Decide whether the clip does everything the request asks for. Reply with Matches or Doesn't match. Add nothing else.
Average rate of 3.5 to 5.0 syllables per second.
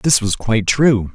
Matches